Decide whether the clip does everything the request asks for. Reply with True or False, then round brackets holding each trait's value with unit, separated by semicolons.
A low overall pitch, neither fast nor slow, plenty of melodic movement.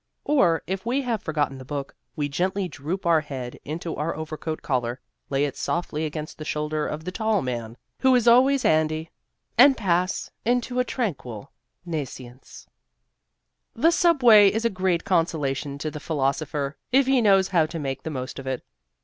False (160 Hz; 175 wpm; 6.2 semitones)